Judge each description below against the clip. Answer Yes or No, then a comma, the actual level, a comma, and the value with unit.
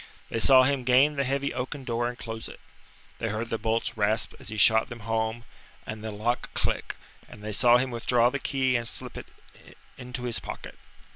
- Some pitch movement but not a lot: No, narrow, 2.3 semitones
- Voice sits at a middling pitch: No, low, 120 Hz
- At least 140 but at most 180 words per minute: No, fast, 205 wpm